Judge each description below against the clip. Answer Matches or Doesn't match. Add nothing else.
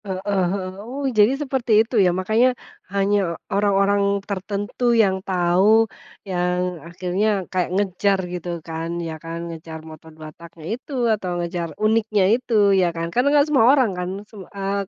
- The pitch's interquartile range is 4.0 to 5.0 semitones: Doesn't match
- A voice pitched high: Matches